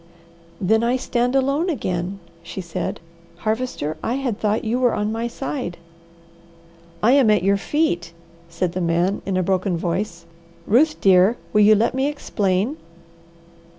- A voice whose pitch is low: No, high, 210 Hz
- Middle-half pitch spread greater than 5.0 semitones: Yes, wide, 5.4 semitones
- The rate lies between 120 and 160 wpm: Yes, average, 150 wpm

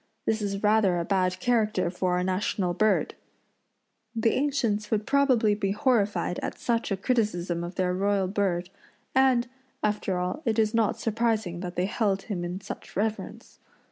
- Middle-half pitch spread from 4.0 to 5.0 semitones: No, average, 3.4 semitones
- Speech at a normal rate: Yes, average, 165 wpm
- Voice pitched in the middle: No, high, 205 Hz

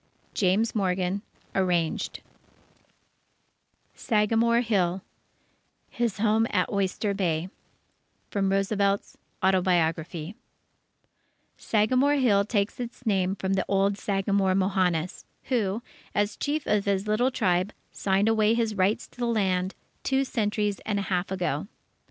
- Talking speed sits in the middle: No, slow, 115 wpm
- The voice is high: Yes, high, 200 Hz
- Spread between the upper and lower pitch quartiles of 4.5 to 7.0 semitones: No, average, 2.7 semitones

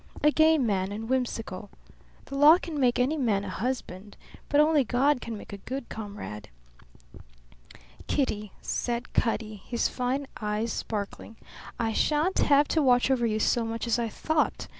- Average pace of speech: Yes, average, 160 wpm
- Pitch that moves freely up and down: No, average, 4.7 semitones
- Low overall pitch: No, high, 240 Hz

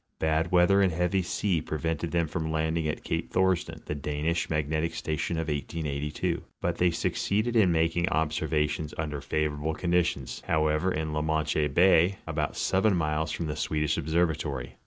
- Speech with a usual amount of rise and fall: No, narrow, 2.1 semitones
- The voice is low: Yes, very low, 80 Hz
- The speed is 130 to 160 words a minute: No, average, 170 wpm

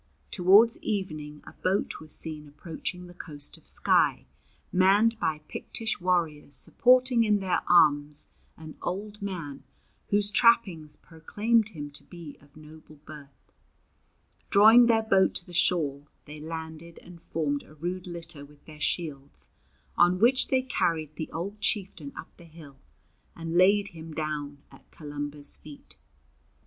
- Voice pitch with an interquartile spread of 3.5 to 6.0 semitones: Yes, average, 4.8 semitones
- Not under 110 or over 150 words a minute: Yes, average, 145 wpm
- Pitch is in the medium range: Yes, medium, 165 Hz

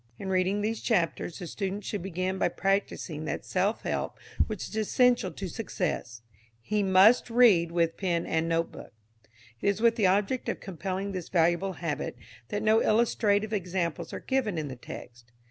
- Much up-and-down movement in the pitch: No, average, 3.7 semitones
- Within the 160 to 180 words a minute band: Yes, average, 170 wpm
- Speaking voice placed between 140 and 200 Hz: Yes, high, 190 Hz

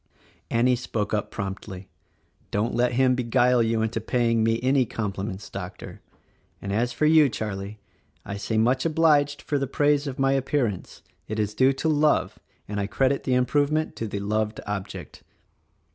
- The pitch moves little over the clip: No, average, 4.3 semitones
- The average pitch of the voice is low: Yes, low, 120 Hz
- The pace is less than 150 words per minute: No, average, 175 wpm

